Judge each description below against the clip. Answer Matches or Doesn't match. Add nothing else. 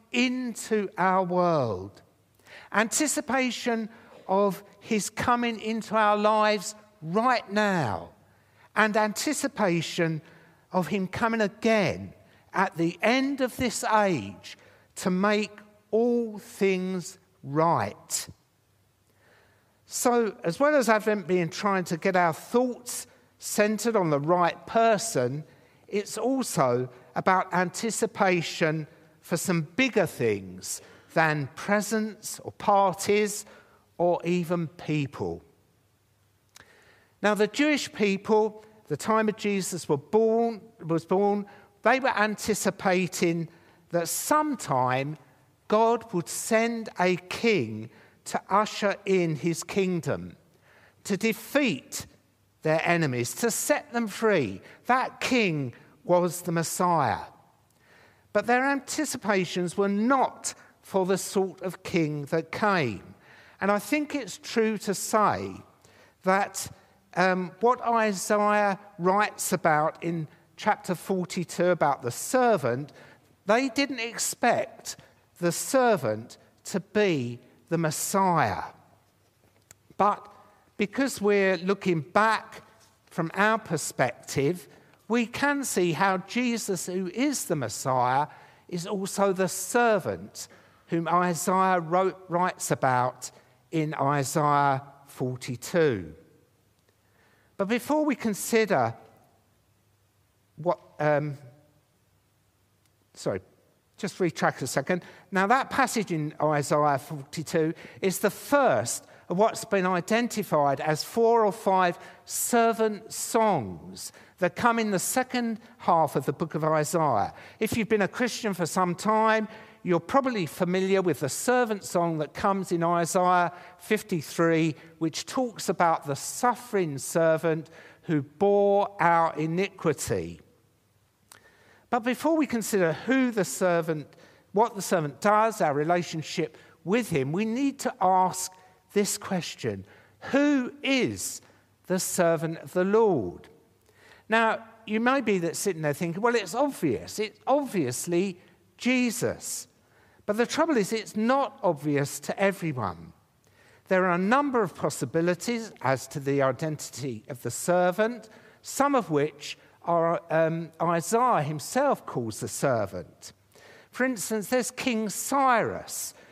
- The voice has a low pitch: Doesn't match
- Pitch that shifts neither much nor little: Doesn't match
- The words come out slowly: Matches